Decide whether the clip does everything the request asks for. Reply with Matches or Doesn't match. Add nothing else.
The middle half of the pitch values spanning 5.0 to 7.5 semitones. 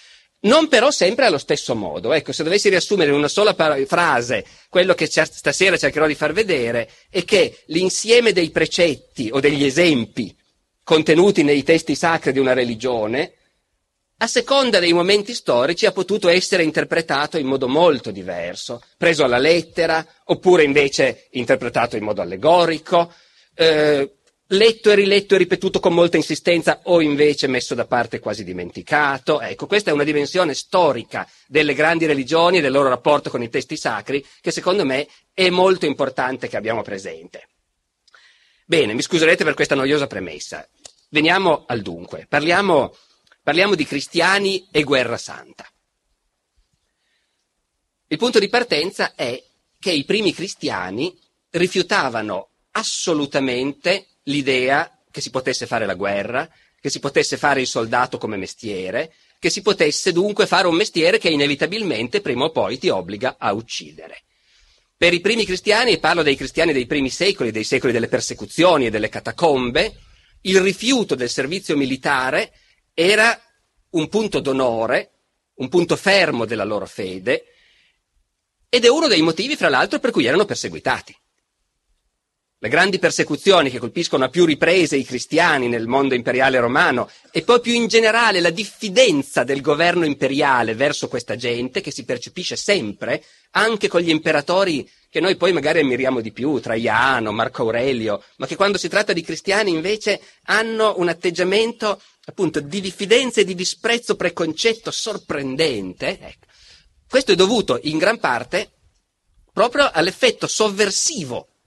Matches